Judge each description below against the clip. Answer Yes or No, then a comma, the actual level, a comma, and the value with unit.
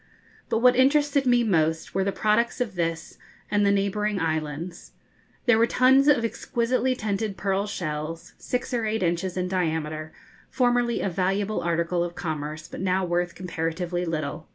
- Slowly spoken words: No, average, 160 wpm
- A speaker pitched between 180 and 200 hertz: Yes, high, 190 Hz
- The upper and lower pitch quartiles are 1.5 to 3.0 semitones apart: No, wide, 5.5 semitones